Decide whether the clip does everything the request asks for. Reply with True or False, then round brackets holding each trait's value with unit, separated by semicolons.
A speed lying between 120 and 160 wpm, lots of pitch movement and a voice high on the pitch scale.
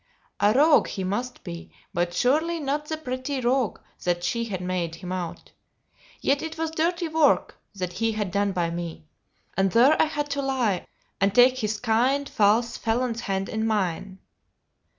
False (170 wpm; 6.6 semitones; 225 Hz)